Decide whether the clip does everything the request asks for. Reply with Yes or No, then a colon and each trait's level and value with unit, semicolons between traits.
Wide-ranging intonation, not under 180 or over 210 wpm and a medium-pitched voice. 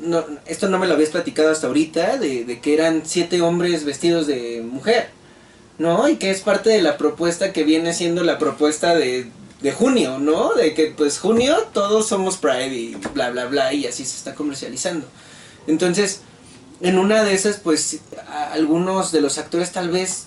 No: average, 3.8 semitones; fast, 190 wpm; medium, 165 Hz